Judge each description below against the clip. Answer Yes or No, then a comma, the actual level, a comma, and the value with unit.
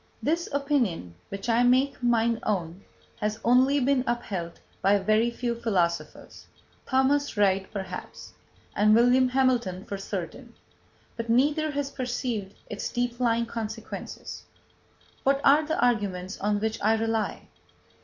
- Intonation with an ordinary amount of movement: Yes, average, 4.2 semitones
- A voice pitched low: No, high, 230 Hz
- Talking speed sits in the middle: No, slow, 130 wpm